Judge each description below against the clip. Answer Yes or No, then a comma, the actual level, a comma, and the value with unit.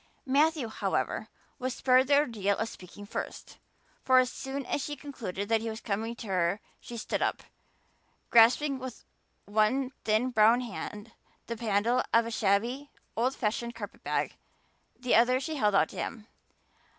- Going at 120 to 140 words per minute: No, average, 165 wpm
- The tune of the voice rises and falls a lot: No, average, 3.4 semitones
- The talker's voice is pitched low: No, high, 235 Hz